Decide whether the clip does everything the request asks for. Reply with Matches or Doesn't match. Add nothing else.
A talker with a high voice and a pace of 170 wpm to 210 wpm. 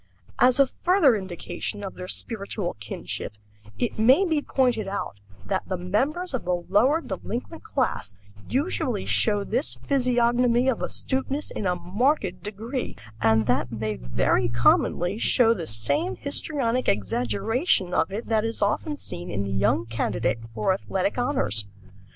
Doesn't match